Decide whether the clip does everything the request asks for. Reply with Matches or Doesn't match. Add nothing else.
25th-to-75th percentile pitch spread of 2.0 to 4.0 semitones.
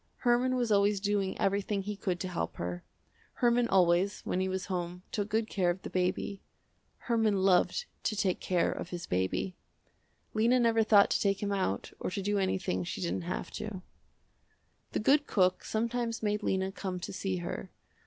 Matches